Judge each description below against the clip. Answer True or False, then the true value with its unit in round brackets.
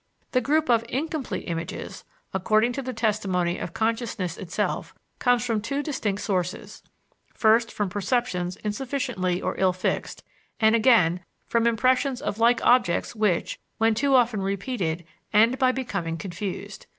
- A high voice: True (220 Hz)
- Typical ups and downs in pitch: True (5.0 semitones)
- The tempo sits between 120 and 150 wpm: True (140 wpm)